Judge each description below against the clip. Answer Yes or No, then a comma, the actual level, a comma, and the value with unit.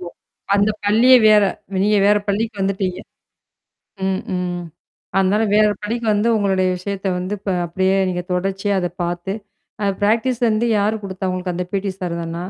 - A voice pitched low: No, high, 195 Hz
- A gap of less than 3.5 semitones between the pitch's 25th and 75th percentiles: Yes, narrow, 2.4 semitones